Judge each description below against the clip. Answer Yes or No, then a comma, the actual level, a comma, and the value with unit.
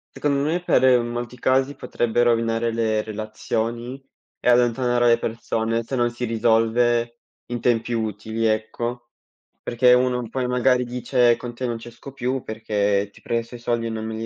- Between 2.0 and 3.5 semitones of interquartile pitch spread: No, narrow, 1.5 semitones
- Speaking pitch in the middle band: No, low, 120 Hz